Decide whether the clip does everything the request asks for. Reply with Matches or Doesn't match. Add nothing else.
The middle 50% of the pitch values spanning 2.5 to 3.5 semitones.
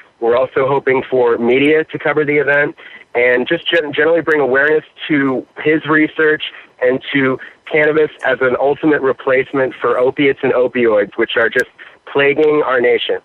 Matches